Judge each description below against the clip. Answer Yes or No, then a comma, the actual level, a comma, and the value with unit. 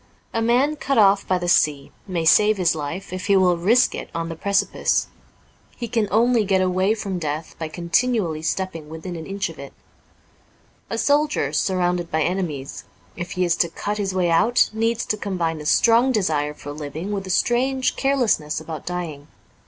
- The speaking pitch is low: No, medium, 185 Hz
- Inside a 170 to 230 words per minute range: Yes, average, 185 wpm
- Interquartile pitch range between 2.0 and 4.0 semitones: No, average, 4.9 semitones